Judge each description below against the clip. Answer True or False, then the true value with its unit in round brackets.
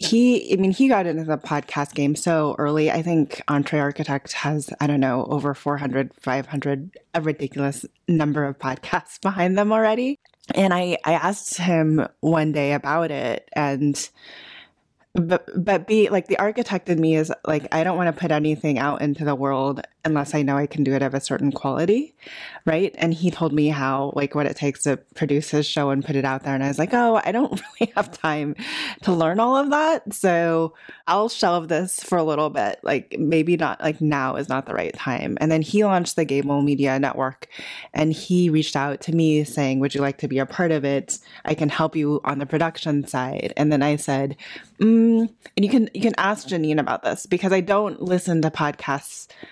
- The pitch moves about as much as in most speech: True (4.1 semitones)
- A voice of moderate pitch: True (155 Hz)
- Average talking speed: False (210 wpm)